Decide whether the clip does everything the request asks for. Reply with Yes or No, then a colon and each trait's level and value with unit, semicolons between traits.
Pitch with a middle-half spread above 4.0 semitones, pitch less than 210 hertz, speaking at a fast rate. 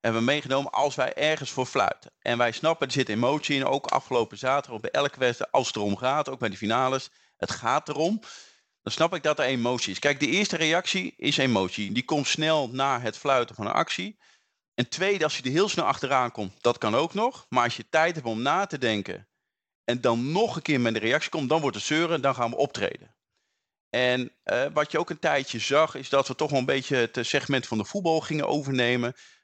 Yes: average, 4.4 semitones; low, 135 Hz; fast, 240 wpm